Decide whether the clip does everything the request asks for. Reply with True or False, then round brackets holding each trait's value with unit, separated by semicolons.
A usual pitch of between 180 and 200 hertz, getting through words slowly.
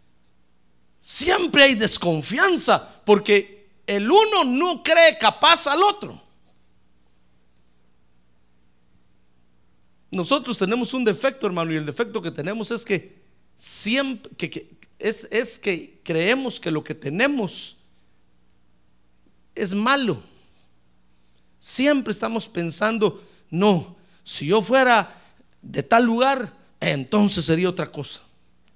True (190 Hz; 105 wpm)